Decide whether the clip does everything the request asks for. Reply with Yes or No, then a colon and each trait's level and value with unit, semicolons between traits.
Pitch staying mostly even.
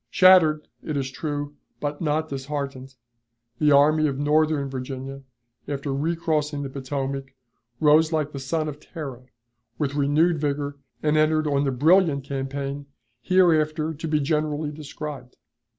Yes: narrow, 1.9 semitones